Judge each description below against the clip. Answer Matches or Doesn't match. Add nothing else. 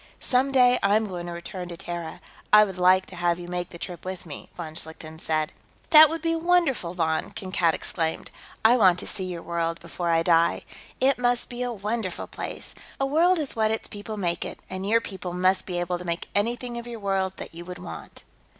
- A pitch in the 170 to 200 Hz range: Matches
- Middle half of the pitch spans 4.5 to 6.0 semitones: Matches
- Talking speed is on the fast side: Matches